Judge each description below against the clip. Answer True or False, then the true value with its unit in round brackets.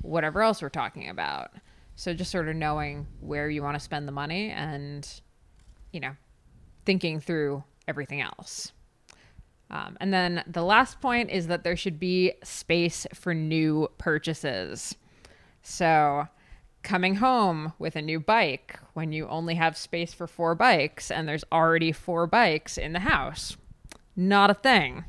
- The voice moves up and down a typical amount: True (3.3 semitones)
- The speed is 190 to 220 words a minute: False (155 wpm)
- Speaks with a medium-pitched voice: True (165 Hz)